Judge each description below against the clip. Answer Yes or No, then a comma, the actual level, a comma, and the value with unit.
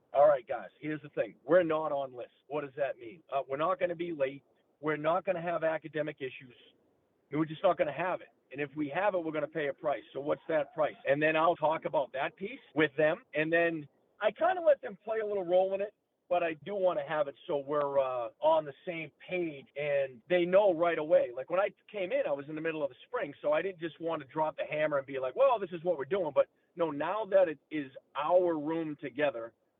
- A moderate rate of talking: No, fast, 270 wpm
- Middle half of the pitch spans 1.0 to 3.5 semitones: No, average, 4.1 semitones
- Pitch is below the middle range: No, medium, 160 Hz